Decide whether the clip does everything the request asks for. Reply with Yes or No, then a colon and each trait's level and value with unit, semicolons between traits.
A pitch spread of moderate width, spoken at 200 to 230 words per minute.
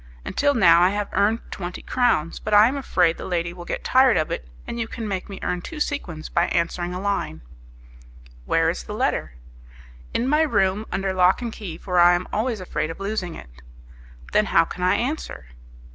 Yes: average, 4.4 semitones; fast, 205 wpm